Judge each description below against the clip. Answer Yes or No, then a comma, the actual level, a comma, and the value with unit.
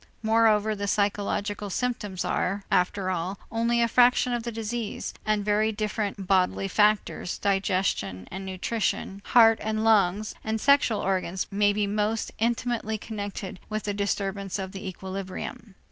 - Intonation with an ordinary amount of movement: No, narrow, 2.2 semitones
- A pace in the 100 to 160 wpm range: Yes, average, 145 wpm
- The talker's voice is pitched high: Yes, high, 205 Hz